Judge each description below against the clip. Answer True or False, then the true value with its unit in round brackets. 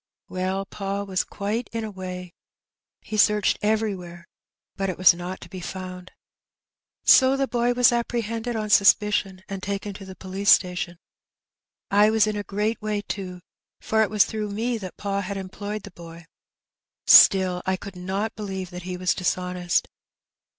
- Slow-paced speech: False (170 wpm)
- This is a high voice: True (195 Hz)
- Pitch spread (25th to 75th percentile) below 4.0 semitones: True (2.5 semitones)